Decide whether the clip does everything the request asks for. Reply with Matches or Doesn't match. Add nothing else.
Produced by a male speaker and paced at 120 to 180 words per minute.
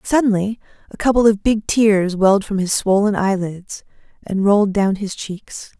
Doesn't match